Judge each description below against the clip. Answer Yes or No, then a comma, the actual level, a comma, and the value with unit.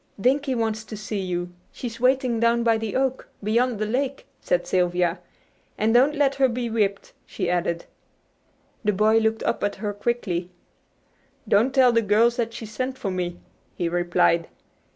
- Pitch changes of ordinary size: Yes, average, 4.0 semitones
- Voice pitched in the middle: No, high, 225 Hz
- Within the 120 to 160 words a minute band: No, average, 170 wpm